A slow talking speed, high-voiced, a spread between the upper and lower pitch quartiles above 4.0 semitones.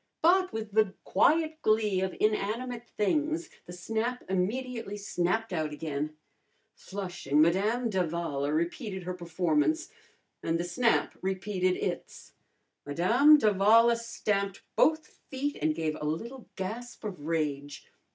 Yes: slow, 120 wpm; high, 200 Hz; wide, 5.5 semitones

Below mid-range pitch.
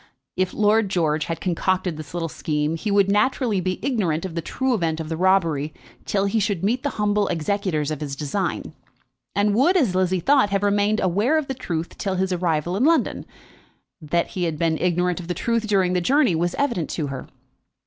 No: medium, 185 Hz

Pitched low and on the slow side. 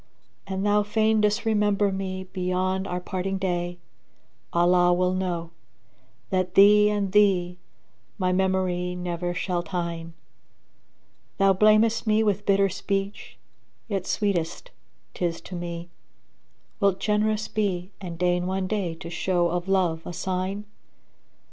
No: medium, 185 Hz; slow, 130 wpm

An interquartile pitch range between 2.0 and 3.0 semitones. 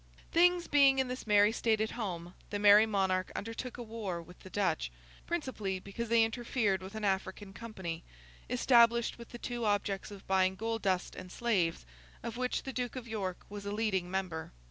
No: average, 3.8 semitones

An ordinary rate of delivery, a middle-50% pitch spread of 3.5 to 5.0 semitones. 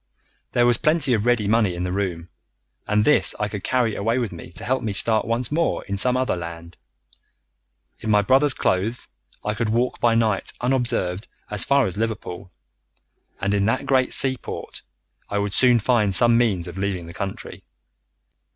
Yes: average, 185 wpm; average, 3.8 semitones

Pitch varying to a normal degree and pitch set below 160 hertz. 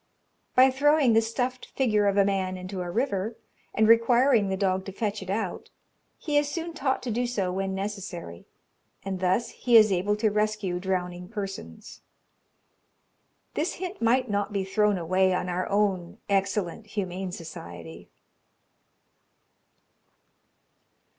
No: average, 3.7 semitones; high, 200 Hz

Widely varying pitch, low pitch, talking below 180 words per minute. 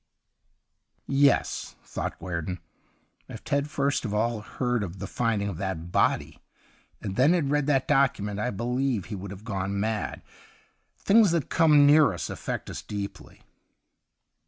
Yes: wide, 6.0 semitones; low, 115 Hz; average, 165 wpm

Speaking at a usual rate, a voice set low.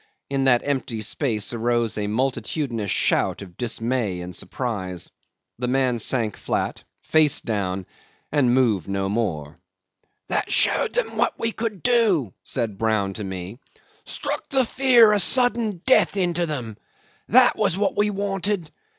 Yes: average, 145 wpm; low, 125 Hz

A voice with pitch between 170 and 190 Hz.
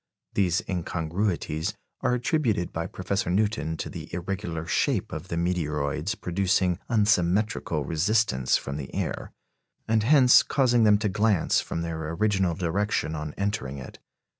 No: very low, 90 Hz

